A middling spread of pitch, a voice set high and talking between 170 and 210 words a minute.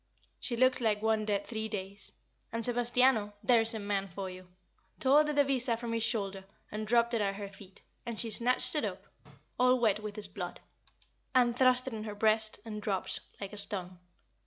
Yes: average, 3.0 semitones; high, 220 Hz; average, 200 wpm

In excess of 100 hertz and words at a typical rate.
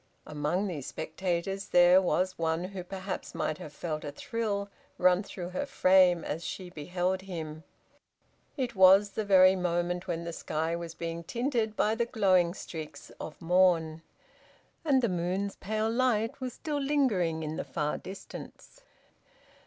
Yes: medium, 185 Hz; average, 155 wpm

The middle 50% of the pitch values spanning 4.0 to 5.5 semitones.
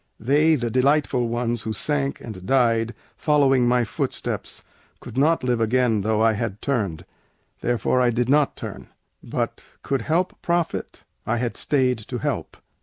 No: average, 3.4 semitones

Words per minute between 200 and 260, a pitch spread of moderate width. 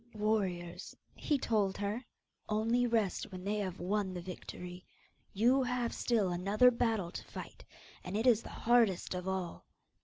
No: average, 155 wpm; average, 4.0 semitones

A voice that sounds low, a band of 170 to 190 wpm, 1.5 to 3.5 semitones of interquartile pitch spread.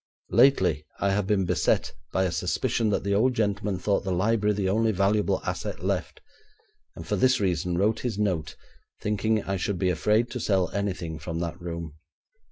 Yes: low, 100 Hz; average, 180 wpm; average, 3.0 semitones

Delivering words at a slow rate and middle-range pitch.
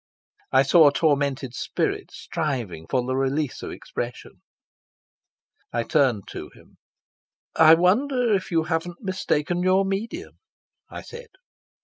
Yes: slow, 125 wpm; medium, 160 Hz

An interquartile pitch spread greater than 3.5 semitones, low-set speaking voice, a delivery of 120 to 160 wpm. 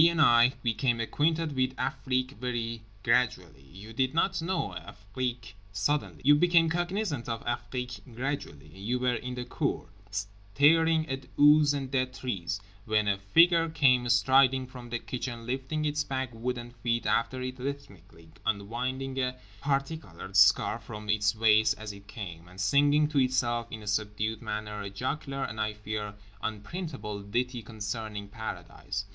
Yes: average, 4.4 semitones; low, 120 Hz; average, 150 wpm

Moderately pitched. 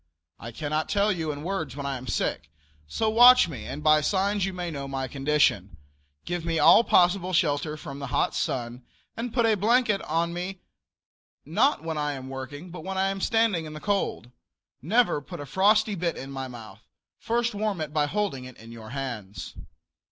Yes: medium, 160 Hz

